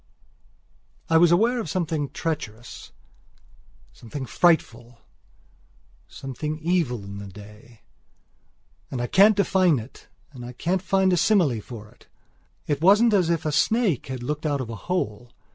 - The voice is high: No, medium, 150 Hz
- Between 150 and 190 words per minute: No, average, 140 wpm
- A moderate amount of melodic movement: No, wide, 7.0 semitones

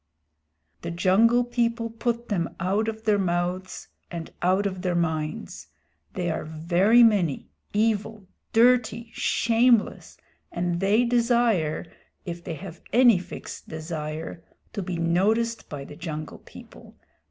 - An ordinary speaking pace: No, slow, 130 wpm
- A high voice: Yes, high, 195 Hz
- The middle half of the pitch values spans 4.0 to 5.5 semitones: Yes, average, 5.1 semitones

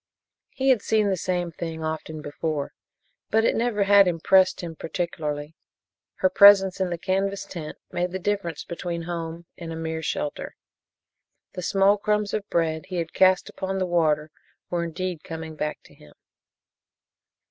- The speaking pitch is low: No, medium, 175 Hz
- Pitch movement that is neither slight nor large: Yes, average, 3.2 semitones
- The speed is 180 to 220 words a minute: No, average, 160 wpm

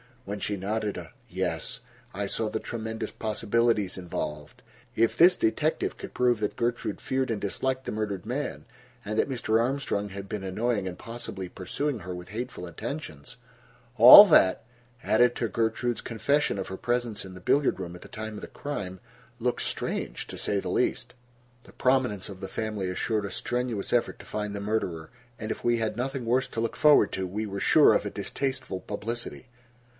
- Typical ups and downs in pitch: Yes, average, 3.7 semitones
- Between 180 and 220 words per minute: Yes, average, 185 wpm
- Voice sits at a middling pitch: No, low, 110 Hz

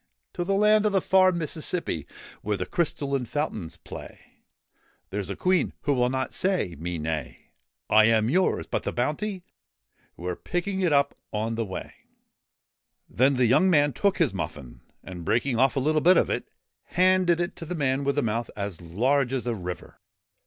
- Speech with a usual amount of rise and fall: No, wide, 8.6 semitones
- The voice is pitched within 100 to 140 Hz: Yes, low, 135 Hz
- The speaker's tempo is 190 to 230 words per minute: Yes, average, 200 wpm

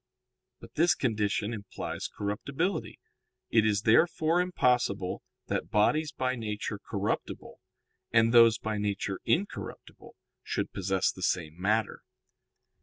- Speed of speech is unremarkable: No, slow, 110 wpm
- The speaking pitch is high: No, low, 110 Hz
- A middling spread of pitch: Yes, average, 4.4 semitones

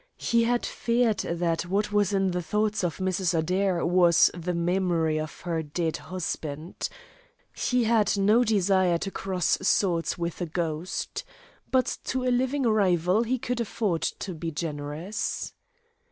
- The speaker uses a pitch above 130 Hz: Yes, medium, 185 Hz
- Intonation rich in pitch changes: No, average, 3.9 semitones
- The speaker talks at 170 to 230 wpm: No, average, 150 wpm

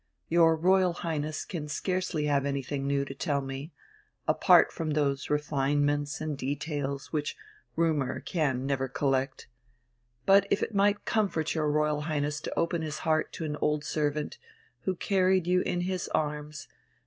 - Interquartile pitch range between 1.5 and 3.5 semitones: Yes, average, 2.8 semitones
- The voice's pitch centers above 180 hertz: No, medium, 150 Hz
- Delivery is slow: No, average, 155 wpm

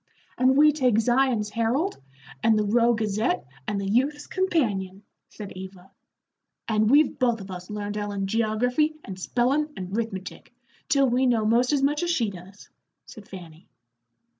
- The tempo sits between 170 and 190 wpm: No, average, 160 wpm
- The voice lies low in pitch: No, high, 225 Hz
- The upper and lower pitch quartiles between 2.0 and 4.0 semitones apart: No, average, 4.7 semitones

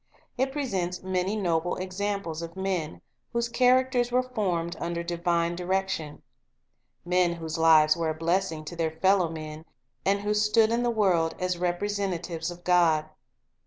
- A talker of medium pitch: Yes, medium, 180 Hz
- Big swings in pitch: No, average, 3.5 semitones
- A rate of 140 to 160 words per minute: Yes, average, 155 wpm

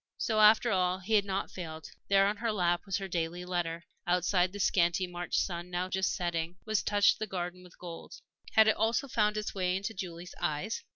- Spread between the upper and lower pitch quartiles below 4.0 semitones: Yes, average, 2.8 semitones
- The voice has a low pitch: No, medium, 185 Hz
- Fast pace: Yes, fast, 210 wpm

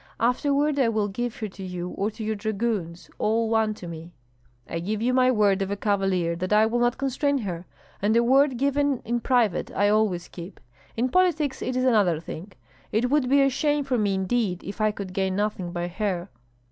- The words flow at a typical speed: No, fast, 210 wpm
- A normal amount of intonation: Yes, average, 4.7 semitones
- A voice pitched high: Yes, high, 215 Hz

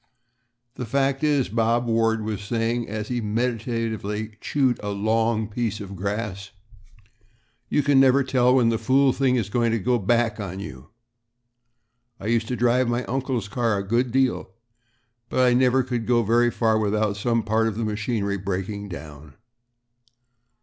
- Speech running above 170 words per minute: No, average, 165 wpm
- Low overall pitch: Yes, low, 115 Hz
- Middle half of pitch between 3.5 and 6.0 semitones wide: No, average, 2.9 semitones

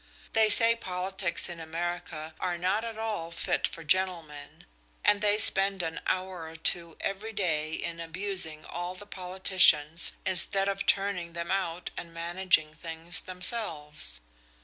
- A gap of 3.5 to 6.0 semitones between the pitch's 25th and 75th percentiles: No, average, 2.8 semitones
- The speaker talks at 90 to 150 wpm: Yes, average, 145 wpm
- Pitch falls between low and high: Yes, medium, 180 Hz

